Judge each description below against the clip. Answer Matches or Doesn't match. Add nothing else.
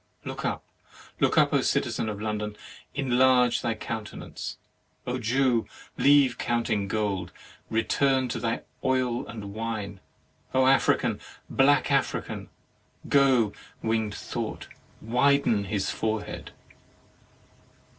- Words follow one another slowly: Matches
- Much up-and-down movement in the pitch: Doesn't match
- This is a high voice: Doesn't match